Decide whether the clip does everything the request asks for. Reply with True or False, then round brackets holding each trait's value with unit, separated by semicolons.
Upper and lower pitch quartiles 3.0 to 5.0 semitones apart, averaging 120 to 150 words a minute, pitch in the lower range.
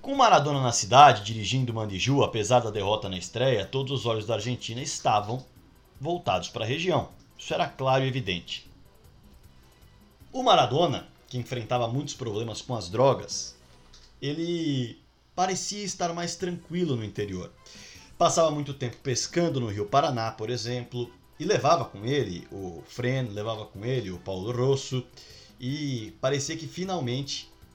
True (4.7 semitones; 145 wpm; 125 Hz)